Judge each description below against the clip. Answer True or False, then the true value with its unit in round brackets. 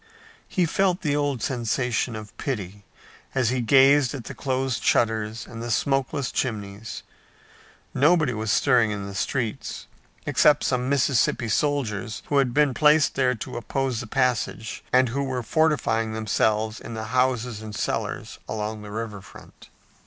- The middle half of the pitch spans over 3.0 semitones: True (3.7 semitones)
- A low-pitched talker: True (125 Hz)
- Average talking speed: True (155 wpm)